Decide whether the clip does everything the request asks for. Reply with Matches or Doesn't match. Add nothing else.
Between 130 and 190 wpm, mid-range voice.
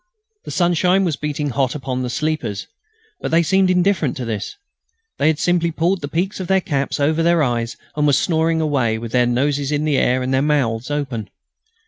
Doesn't match